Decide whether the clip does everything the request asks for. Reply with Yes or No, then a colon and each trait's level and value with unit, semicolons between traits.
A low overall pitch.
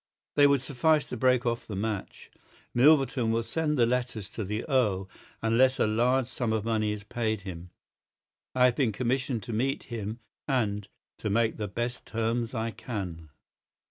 Yes: low, 115 Hz